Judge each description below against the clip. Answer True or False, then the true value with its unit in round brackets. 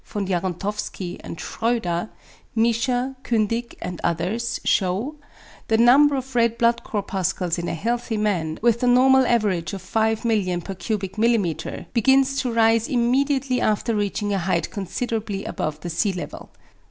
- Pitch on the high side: True (220 Hz)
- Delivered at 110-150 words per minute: True (140 wpm)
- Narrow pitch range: False (4.1 semitones)